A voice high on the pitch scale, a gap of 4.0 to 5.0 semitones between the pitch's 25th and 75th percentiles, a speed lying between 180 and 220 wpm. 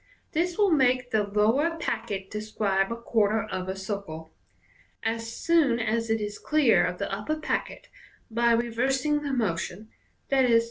No: high, 230 Hz; average, 4.3 semitones; average, 155 wpm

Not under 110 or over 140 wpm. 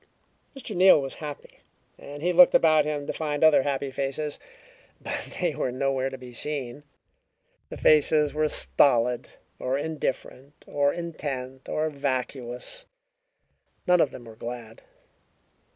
Yes: slow, 135 wpm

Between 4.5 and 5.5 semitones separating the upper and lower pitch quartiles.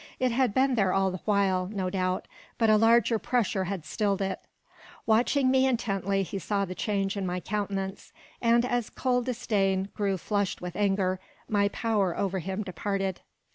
No: average, 3.0 semitones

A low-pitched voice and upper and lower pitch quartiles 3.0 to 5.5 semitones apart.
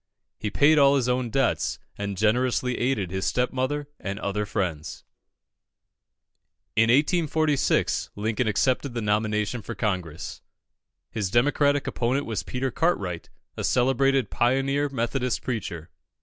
Yes: low, 120 Hz; average, 4.6 semitones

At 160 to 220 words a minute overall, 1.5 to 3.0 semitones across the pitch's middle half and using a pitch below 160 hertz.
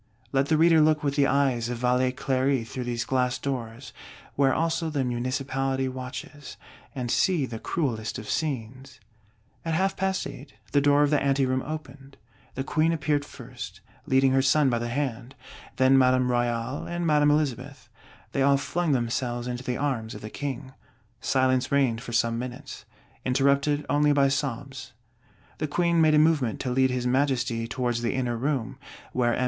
Yes: average, 175 wpm; average, 2.7 semitones; low, 135 Hz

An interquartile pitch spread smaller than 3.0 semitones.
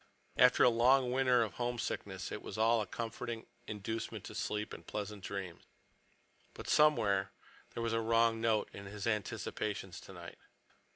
Yes: narrow, 2.4 semitones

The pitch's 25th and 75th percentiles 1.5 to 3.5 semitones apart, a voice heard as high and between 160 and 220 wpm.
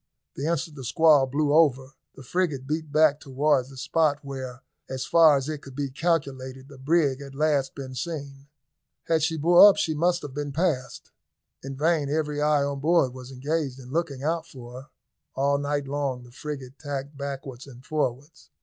No: narrow, 2.6 semitones; medium, 140 Hz; average, 185 wpm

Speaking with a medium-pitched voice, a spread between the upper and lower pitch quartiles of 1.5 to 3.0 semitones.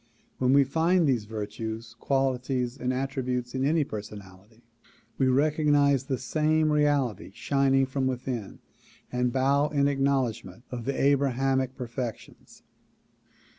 No: low, 130 Hz; narrow, 2.6 semitones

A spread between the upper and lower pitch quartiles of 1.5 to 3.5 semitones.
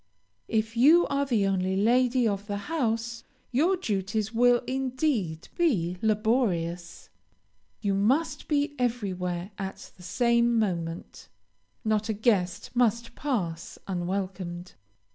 No: average, 4.6 semitones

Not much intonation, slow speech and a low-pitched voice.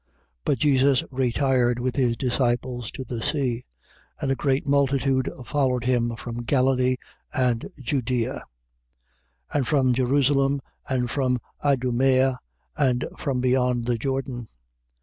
Yes: narrow, 1.8 semitones; slow, 130 wpm; low, 130 Hz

